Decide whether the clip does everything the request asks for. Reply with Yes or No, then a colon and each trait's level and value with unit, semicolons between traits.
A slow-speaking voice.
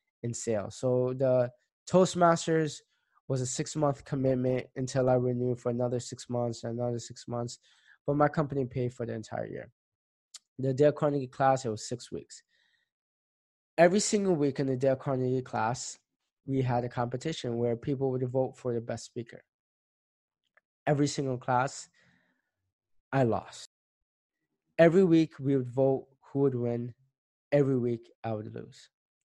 No: average, 150 wpm